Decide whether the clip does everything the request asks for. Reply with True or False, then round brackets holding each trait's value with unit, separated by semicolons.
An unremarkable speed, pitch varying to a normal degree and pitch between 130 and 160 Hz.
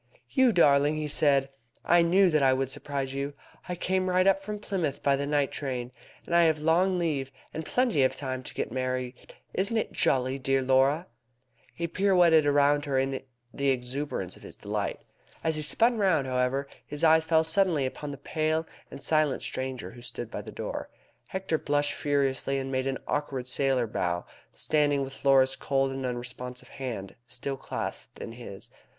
True (185 wpm; 3.5 semitones; 140 Hz)